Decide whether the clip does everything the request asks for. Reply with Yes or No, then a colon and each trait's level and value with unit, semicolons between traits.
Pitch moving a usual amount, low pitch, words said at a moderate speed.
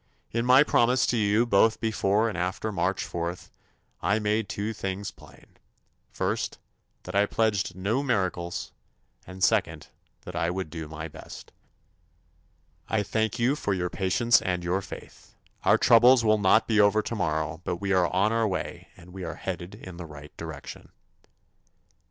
Yes: average, 3.9 semitones; low, 100 Hz; average, 165 wpm